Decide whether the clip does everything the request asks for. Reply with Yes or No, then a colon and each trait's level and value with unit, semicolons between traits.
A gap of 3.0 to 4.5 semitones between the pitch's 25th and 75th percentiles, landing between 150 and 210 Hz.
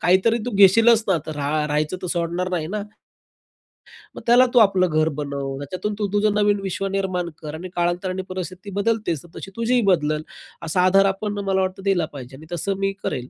Yes: average, 3.9 semitones; medium, 185 Hz